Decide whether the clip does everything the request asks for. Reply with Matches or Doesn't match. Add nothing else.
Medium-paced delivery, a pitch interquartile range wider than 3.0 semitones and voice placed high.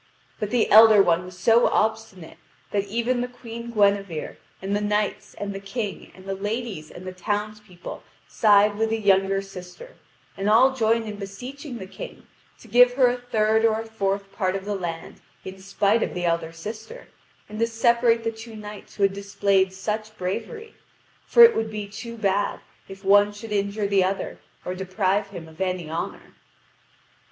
Doesn't match